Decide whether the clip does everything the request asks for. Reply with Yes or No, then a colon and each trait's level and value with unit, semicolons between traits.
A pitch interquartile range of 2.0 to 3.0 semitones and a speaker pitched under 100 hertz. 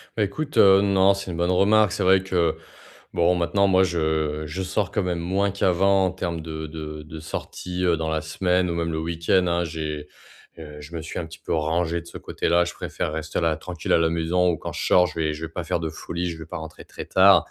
Yes: narrow, 2.6 semitones; very low, 85 Hz